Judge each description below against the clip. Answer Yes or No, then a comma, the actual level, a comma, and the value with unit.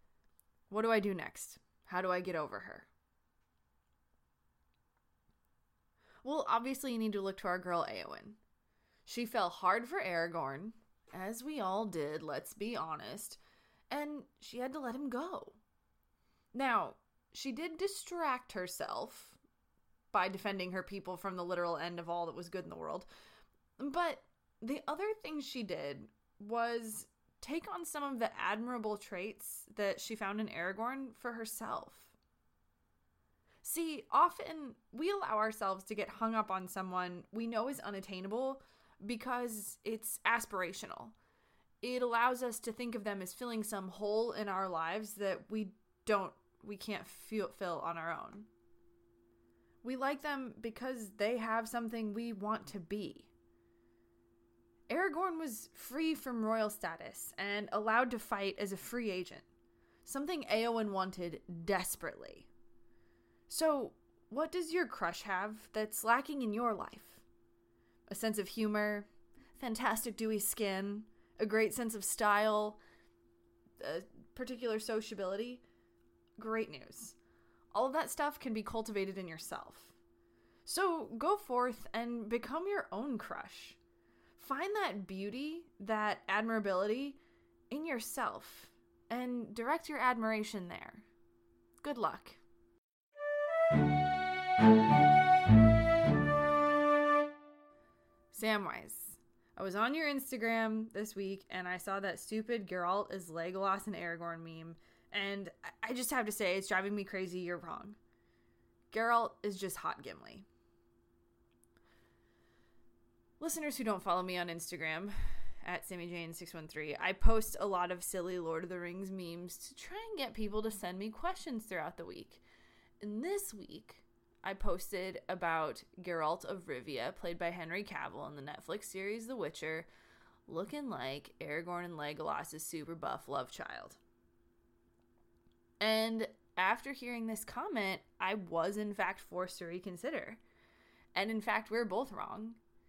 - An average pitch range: No, wide, 5.7 semitones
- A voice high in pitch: Yes, high, 205 Hz